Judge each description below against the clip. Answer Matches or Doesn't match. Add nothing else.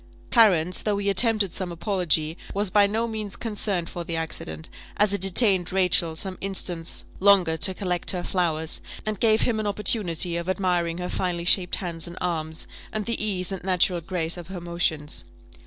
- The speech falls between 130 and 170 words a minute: Doesn't match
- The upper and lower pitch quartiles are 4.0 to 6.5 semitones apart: Doesn't match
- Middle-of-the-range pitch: Matches